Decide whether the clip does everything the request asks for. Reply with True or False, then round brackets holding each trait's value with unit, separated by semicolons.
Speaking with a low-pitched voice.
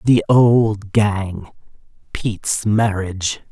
True (105 Hz)